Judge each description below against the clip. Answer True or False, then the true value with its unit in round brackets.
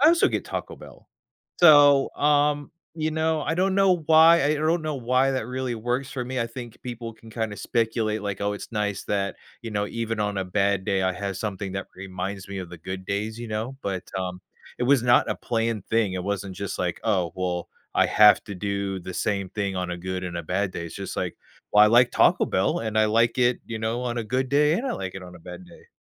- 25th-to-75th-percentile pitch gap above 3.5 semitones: True (4.9 semitones)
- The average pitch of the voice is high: False (110 Hz)